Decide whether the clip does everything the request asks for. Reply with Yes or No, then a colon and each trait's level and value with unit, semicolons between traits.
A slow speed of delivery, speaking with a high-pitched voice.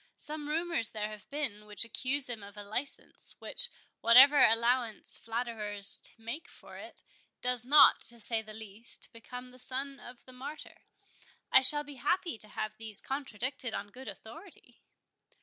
No: average, 155 wpm; high, 245 Hz